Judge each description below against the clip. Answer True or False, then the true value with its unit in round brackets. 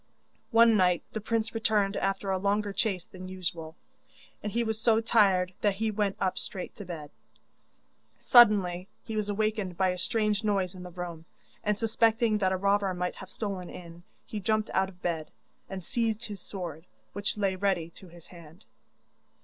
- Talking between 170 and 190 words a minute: True (180 wpm)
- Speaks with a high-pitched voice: True (195 Hz)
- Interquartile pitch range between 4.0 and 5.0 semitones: False (2.9 semitones)